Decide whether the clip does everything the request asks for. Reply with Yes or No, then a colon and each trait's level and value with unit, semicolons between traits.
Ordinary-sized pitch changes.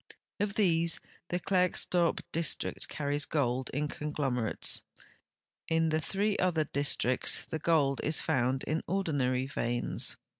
Yes: average, 3.9 semitones